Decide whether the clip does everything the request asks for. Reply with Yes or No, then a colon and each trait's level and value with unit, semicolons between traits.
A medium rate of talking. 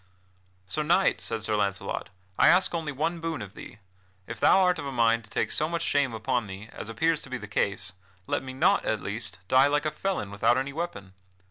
No: fast, 225 wpm